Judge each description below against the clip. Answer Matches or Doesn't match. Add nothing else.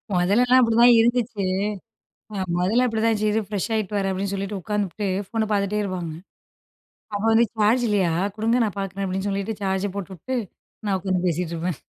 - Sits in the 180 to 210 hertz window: Matches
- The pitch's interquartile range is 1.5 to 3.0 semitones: Matches